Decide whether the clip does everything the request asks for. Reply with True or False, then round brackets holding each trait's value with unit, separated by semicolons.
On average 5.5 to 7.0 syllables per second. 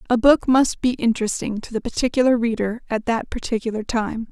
True (5.7 syllables/s)